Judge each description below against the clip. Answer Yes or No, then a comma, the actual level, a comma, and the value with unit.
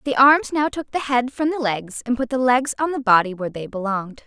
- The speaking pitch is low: No, very high, 250 Hz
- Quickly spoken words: Yes, fast, 265 wpm